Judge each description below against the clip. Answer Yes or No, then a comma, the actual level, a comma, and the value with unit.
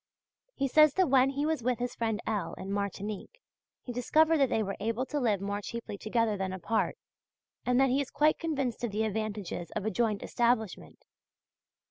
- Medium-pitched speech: No, high, 230 Hz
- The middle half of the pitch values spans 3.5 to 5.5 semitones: Yes, average, 4.5 semitones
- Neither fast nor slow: Yes, average, 190 wpm